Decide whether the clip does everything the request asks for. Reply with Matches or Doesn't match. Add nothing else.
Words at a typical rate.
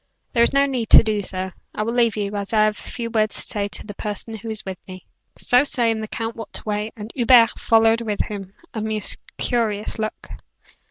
Doesn't match